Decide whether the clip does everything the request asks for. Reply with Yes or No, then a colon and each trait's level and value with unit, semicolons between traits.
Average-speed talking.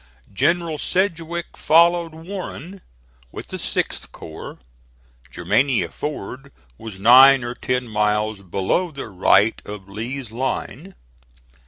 No: slow, 110 wpm